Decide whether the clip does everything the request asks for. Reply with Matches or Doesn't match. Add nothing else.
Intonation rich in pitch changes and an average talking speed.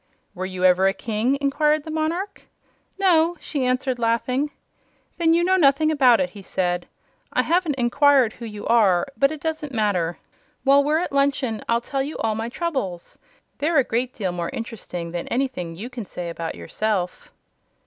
Matches